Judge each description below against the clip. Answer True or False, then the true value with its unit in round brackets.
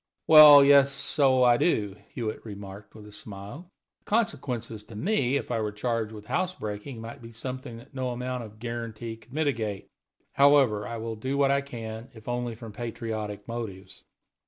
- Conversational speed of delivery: True (180 wpm)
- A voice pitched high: False (115 Hz)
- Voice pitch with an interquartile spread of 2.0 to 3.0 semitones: False (3.8 semitones)